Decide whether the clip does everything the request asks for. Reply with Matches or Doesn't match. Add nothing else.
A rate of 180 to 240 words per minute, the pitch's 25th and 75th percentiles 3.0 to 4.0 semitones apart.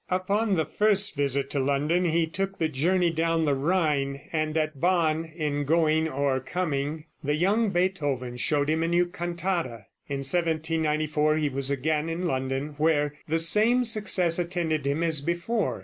Doesn't match